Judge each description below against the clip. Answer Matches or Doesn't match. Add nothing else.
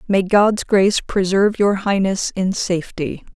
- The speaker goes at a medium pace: Matches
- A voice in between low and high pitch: Doesn't match